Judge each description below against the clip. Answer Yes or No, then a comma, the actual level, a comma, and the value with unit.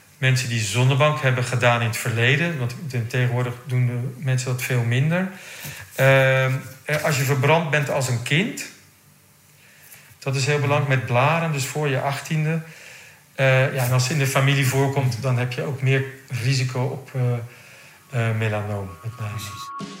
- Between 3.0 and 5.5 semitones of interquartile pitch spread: No, narrow, 2.5 semitones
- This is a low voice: Yes, low, 130 Hz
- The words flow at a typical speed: Yes, average, 165 wpm